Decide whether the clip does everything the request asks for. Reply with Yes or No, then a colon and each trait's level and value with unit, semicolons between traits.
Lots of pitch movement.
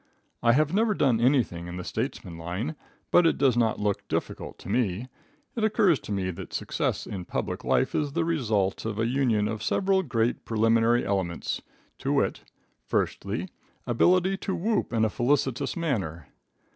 Yes: wide, 6.8 semitones